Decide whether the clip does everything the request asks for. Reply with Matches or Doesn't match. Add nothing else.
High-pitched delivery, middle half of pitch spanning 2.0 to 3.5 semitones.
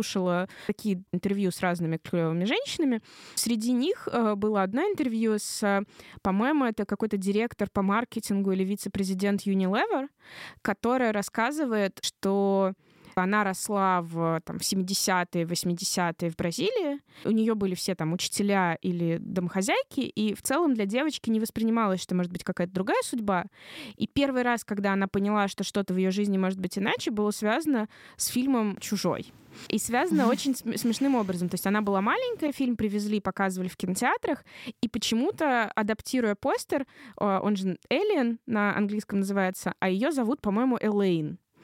Doesn't match